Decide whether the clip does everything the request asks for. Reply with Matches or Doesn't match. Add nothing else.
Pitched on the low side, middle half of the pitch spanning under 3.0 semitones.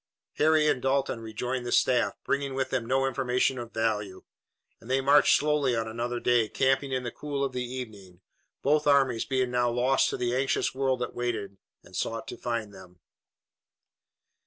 Matches